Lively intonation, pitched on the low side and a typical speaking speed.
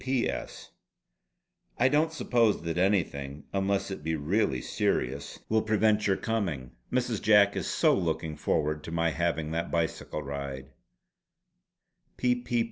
No: wide, 5.9 semitones; very low, 85 Hz; slow, 125 wpm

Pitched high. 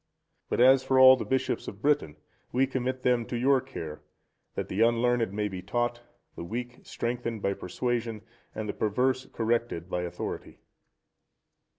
No: low, 120 Hz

